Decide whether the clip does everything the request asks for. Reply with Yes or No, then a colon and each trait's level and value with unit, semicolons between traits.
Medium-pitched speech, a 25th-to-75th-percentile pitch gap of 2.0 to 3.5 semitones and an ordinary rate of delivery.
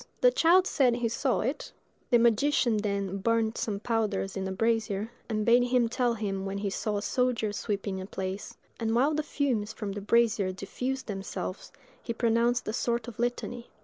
No: high, 225 Hz; average, 3.1 semitones; average, 185 wpm